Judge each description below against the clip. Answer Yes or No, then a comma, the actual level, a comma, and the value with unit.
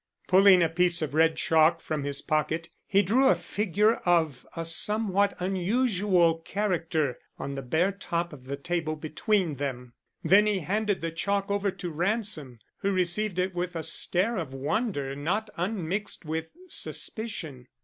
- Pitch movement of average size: Yes, average, 4.2 semitones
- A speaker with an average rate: Yes, average, 160 wpm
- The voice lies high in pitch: No, medium, 175 Hz